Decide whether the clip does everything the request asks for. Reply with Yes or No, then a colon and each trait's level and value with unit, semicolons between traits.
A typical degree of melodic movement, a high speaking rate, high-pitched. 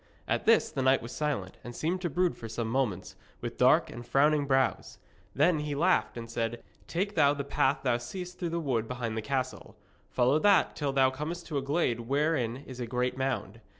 No: average, 4.2 semitones; fast, 210 wpm; low, 135 Hz